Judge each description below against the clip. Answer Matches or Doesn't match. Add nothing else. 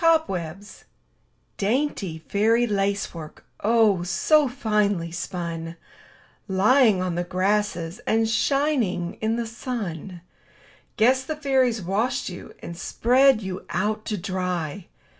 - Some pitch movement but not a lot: Matches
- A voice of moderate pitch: Doesn't match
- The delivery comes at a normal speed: Doesn't match